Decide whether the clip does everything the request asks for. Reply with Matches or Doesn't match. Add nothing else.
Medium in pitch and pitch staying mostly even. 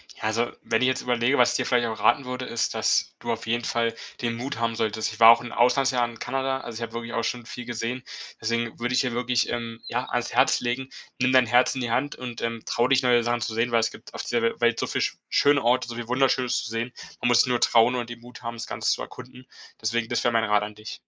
Doesn't match